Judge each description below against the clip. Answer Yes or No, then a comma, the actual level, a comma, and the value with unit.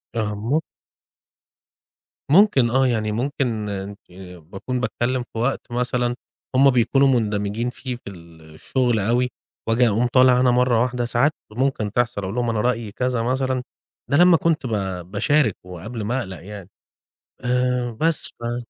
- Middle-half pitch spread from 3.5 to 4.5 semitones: No, average, 3.1 semitones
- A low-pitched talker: Yes, low, 120 Hz